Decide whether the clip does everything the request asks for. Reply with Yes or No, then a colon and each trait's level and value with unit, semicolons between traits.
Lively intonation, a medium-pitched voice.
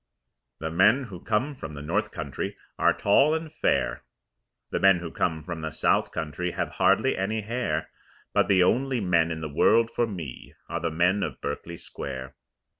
No: wide, 5.7 semitones; very low, 90 Hz